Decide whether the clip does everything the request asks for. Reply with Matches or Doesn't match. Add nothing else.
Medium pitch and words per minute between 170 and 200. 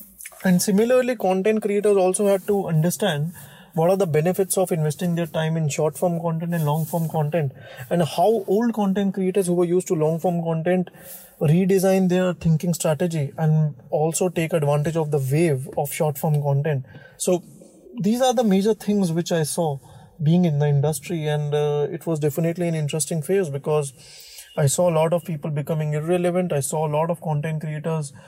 Matches